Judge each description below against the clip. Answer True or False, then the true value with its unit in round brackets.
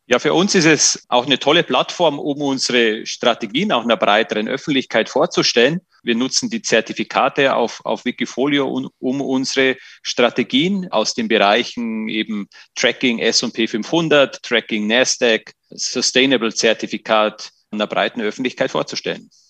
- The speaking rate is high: False (130 wpm)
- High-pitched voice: False (130 Hz)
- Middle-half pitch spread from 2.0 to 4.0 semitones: False (4.5 semitones)